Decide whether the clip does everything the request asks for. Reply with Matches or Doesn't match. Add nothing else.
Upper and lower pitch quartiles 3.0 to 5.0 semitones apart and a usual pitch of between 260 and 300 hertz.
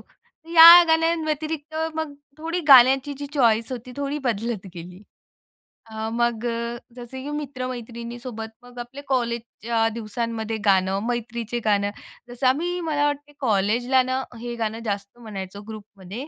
Doesn't match